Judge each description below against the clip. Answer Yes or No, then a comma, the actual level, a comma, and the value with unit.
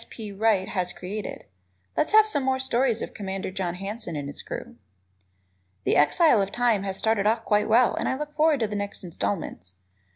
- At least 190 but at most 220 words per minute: Yes, average, 195 wpm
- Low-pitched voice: No, high, 210 Hz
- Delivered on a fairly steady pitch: No, average, 4.3 semitones